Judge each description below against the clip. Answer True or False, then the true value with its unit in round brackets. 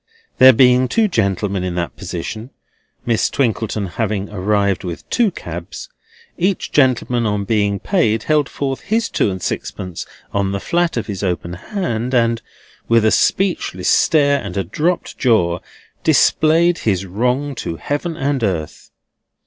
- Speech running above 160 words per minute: False (150 wpm)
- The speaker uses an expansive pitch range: True (6.4 semitones)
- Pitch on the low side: True (115 Hz)